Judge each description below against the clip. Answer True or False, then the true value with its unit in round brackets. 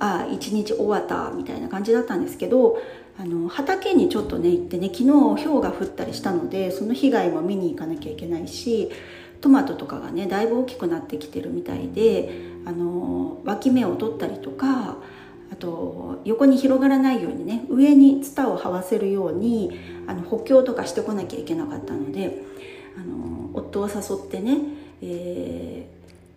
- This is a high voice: True (225 Hz)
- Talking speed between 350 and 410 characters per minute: True (355 characters per minute)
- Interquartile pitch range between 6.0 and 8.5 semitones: True (7.9 semitones)